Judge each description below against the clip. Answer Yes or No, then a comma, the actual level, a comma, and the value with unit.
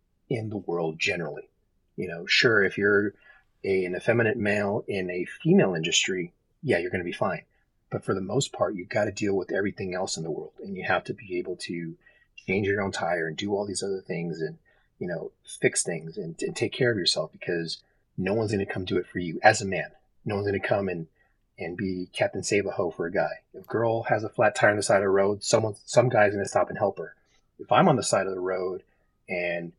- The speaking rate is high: Yes, fast, 250 wpm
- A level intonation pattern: No, average, 3.3 semitones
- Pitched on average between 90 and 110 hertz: Yes, low, 100 Hz